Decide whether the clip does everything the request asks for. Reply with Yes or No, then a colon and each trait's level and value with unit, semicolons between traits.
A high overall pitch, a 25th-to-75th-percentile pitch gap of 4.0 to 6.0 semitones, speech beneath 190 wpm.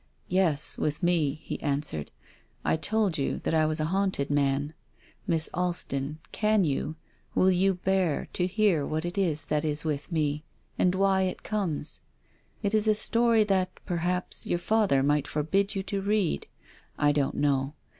No: medium, 170 Hz; average, 4.5 semitones; average, 175 wpm